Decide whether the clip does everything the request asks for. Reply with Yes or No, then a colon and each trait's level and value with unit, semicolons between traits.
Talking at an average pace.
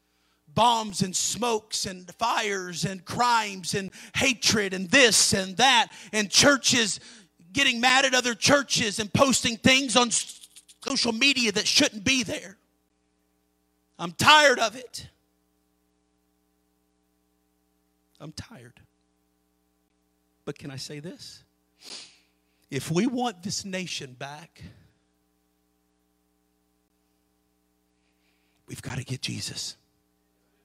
No: slow, 100 wpm